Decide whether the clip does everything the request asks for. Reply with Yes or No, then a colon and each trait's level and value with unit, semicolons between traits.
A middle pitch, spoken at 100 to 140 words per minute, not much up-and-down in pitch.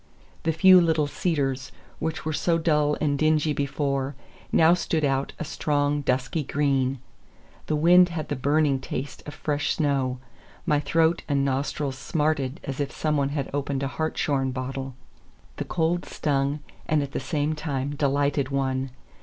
No: medium, 145 Hz; average, 160 wpm; narrow, 2.3 semitones